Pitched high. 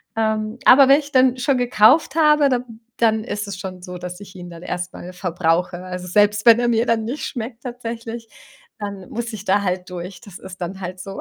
Yes: high, 210 Hz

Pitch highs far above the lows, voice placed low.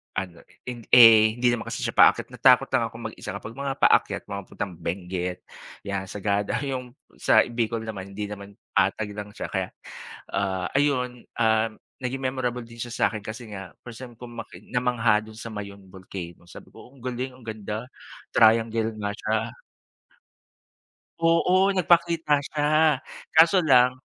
No: average, 3.8 semitones; low, 115 Hz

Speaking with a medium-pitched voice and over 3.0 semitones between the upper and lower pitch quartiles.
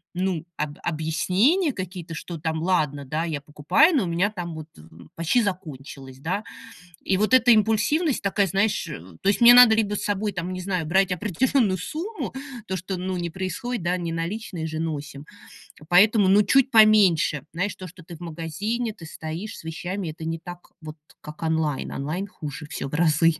Yes: medium, 180 Hz; average, 4.5 semitones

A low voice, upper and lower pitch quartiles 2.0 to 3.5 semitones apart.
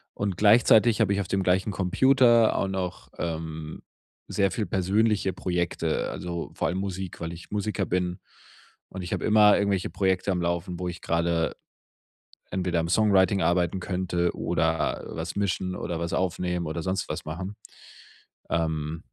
Yes: very low, 90 Hz; narrow, 2.6 semitones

